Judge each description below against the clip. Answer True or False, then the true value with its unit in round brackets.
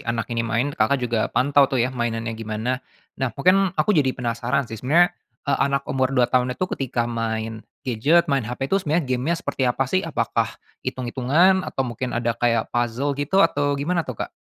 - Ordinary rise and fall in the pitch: True (3.5 semitones)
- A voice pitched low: True (130 Hz)